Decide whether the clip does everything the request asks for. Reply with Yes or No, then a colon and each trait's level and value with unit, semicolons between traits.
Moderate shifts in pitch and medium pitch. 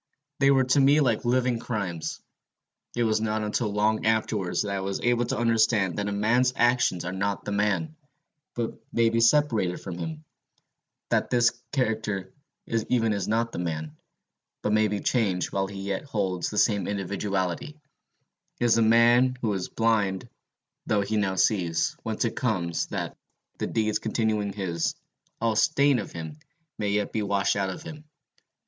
No: average, 3.4 semitones; low, 110 Hz